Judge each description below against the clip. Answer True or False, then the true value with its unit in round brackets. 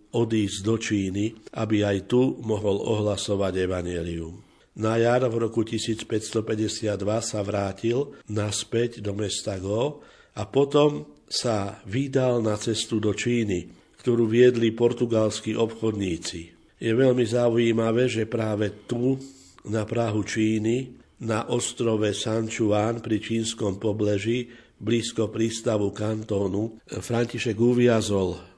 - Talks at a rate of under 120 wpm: True (110 wpm)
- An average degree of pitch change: False (2.1 semitones)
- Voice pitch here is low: True (110 Hz)